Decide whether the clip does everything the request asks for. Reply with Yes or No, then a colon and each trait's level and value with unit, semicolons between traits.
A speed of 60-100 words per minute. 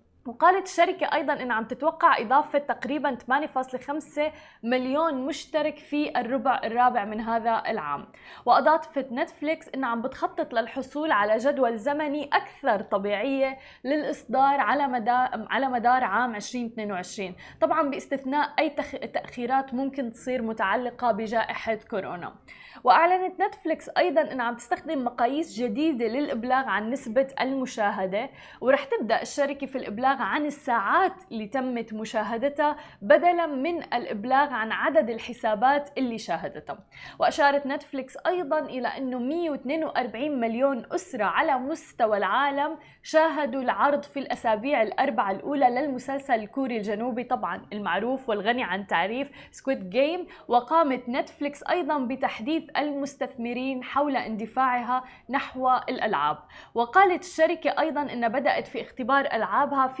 No: average, 120 wpm